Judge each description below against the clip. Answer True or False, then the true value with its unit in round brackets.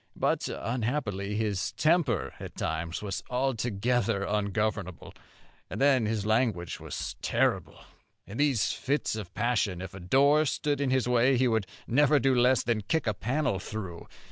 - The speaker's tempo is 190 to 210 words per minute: False (155 wpm)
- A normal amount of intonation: True (4.6 semitones)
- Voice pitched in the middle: False (115 Hz)